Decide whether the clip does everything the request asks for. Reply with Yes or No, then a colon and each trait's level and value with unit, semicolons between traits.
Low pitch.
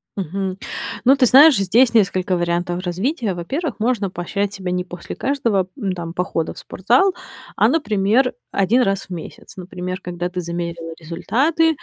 No: high, 190 Hz